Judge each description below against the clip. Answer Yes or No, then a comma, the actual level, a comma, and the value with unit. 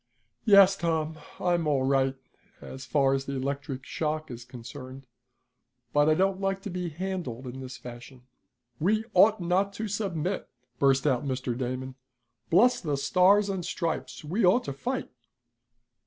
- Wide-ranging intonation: Yes, wide, 6.1 semitones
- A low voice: No, medium, 155 Hz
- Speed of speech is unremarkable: Yes, average, 155 wpm